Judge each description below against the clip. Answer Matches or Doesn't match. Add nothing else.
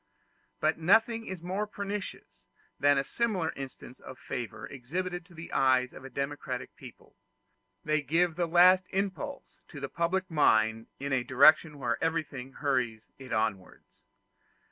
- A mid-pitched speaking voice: Matches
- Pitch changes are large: Matches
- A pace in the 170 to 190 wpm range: Doesn't match